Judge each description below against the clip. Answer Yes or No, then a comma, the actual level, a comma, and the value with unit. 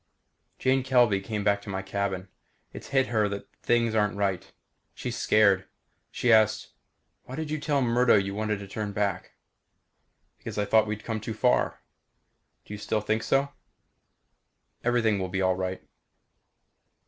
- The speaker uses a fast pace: No, average, 155 wpm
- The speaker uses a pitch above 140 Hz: No, low, 105 Hz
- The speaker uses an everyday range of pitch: Yes, average, 3.1 semitones